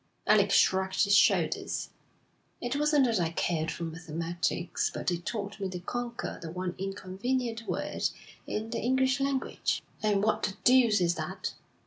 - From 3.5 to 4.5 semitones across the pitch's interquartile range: No, wide, 5.5 semitones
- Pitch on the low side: No, high, 200 Hz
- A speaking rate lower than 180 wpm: Yes, average, 155 wpm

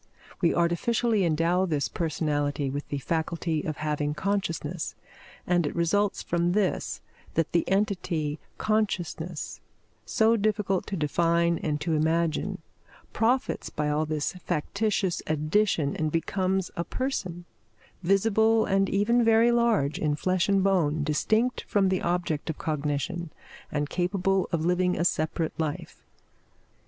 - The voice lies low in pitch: No, medium, 170 Hz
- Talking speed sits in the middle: No, slow, 130 wpm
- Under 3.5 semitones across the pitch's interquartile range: No, average, 4.2 semitones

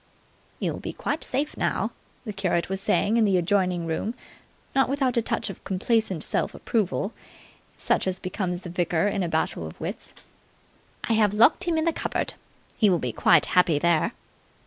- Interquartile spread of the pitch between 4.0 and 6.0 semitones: Yes, average, 4.5 semitones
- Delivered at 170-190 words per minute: Yes, average, 180 wpm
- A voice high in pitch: Yes, high, 195 Hz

